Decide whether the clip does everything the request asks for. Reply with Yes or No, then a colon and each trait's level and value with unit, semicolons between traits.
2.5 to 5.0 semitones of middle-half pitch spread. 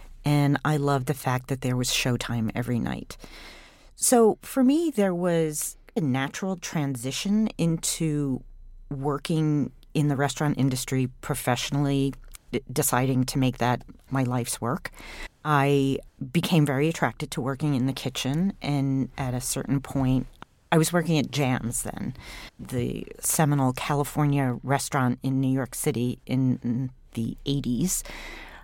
Yes: average, 2.9 semitones